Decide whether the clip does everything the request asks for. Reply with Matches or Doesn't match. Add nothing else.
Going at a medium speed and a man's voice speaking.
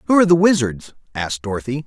Matches